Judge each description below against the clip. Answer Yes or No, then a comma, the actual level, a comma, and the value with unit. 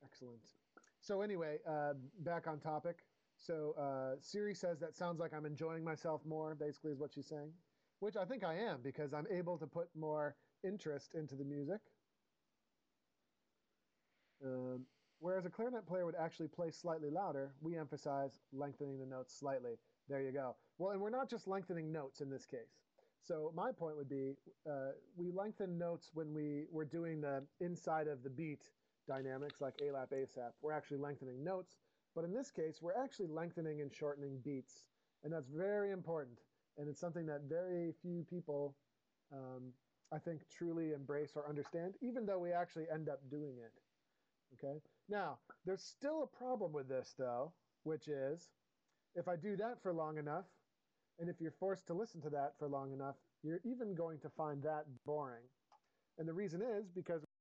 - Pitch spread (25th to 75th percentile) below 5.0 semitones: Yes, average, 3.5 semitones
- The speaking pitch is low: No, medium, 155 Hz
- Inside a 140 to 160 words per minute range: No, average, 180 wpm